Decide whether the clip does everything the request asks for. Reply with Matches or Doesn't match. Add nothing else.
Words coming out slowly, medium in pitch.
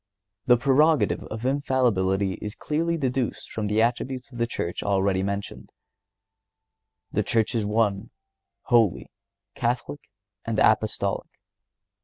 Doesn't match